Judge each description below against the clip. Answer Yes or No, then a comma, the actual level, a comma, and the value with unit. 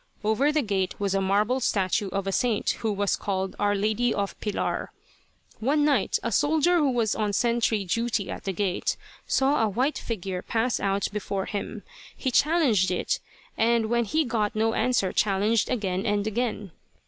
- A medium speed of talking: Yes, average, 175 wpm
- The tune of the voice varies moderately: Yes, average, 3.6 semitones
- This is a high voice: Yes, high, 215 Hz